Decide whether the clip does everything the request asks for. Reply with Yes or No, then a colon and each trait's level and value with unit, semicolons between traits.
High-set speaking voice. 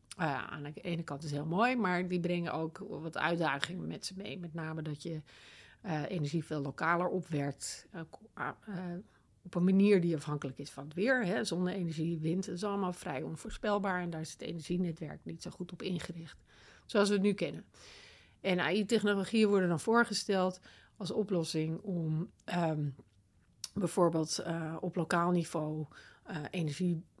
No: medium, 175 Hz